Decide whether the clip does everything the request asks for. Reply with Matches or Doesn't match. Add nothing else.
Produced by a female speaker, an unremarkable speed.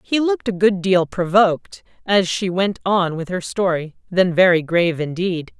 Matches